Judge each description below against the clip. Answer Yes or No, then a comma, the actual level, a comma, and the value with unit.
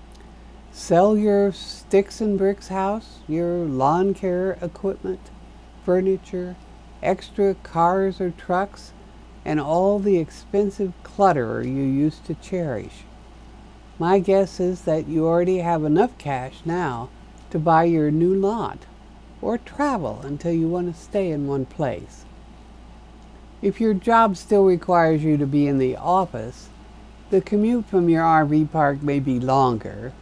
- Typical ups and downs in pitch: Yes, average, 4.5 semitones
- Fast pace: No, slow, 135 wpm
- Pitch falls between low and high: Yes, medium, 175 Hz